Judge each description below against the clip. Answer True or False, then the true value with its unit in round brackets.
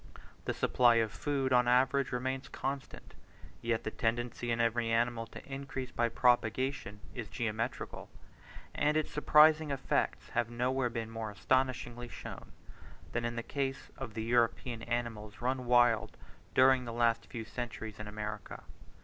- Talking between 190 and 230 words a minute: False (150 wpm)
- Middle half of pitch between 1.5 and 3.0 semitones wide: True (2.4 semitones)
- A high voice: False (120 Hz)